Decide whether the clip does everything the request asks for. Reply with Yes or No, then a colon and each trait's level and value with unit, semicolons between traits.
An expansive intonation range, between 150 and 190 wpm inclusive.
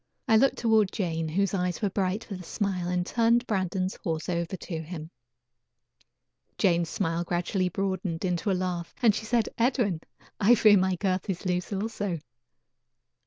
No: average, 3.0 semitones; average, 165 wpm